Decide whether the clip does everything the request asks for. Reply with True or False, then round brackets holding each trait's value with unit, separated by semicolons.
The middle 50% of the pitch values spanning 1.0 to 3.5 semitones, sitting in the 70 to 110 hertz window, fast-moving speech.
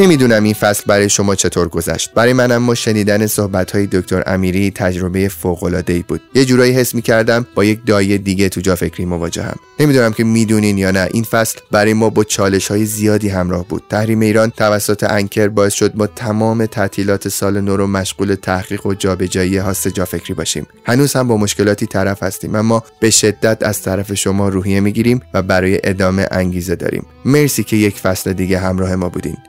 True (2.8 semitones; 100 Hz; 195 wpm)